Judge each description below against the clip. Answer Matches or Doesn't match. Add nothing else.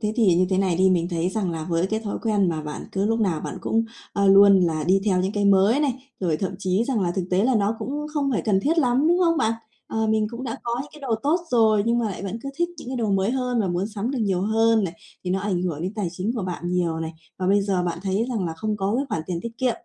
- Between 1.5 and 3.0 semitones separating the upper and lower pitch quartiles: Doesn't match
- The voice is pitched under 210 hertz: Matches